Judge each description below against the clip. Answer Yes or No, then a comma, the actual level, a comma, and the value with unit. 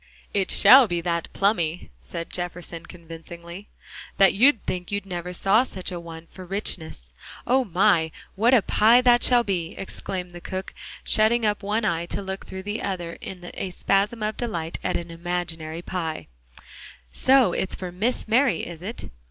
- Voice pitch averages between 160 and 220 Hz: Yes, medium, 185 Hz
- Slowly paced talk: No, average, 170 wpm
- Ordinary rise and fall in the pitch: Yes, average, 3.8 semitones